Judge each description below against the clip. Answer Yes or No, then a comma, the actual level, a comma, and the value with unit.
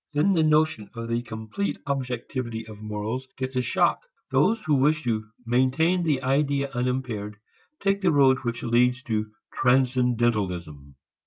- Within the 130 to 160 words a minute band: Yes, average, 145 wpm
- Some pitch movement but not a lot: Yes, average, 3.7 semitones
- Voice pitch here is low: Yes, low, 125 Hz